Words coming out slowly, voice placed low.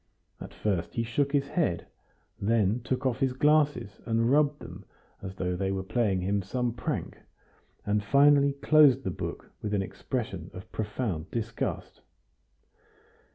No: average, 150 wpm; low, 115 Hz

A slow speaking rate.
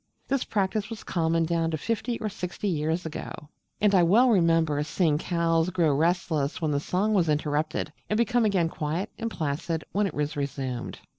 No: average, 180 wpm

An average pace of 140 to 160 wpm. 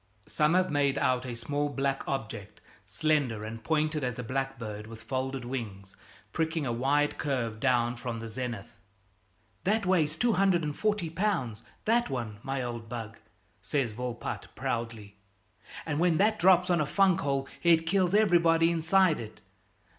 Yes: average, 150 wpm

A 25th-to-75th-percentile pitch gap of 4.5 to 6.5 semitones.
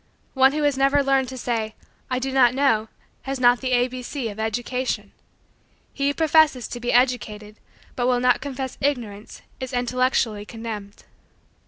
No: average, 2.7 semitones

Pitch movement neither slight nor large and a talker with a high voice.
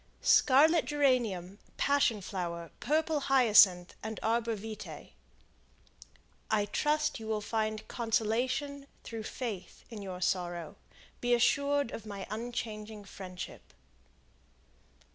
Yes: average, 4.4 semitones; high, 220 Hz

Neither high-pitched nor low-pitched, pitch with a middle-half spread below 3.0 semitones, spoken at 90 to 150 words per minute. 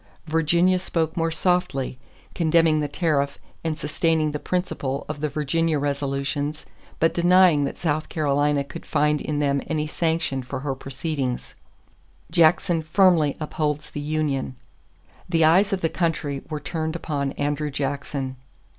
Yes: medium, 150 Hz; narrow, 2.5 semitones; average, 140 wpm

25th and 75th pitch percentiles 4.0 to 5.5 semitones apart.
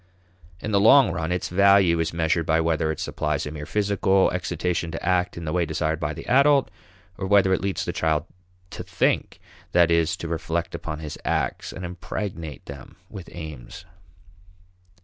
No: average, 2.9 semitones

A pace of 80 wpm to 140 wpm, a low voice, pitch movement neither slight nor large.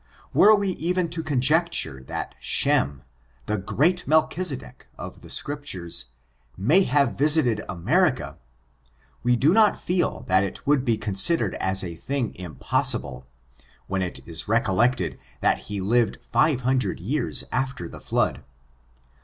No: slow, 135 wpm; low, 125 Hz; wide, 8.4 semitones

